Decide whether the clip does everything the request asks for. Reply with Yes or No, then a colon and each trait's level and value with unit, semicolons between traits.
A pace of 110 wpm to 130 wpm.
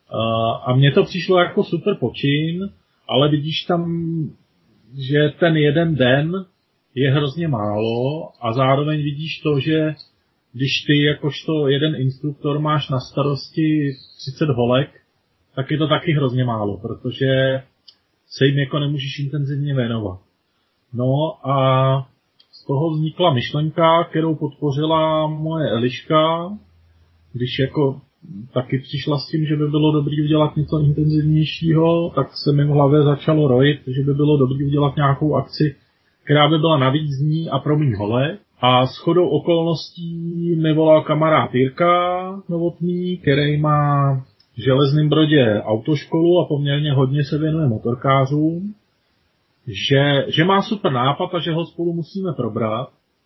No: average, 140 wpm